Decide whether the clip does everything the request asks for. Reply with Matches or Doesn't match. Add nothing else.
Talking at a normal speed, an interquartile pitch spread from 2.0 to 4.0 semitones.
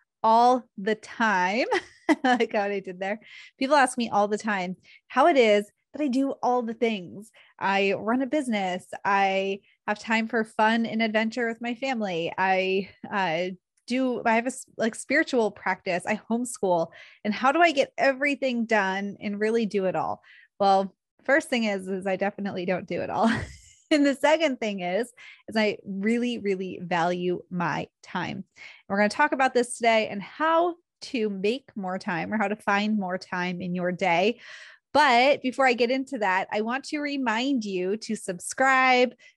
Doesn't match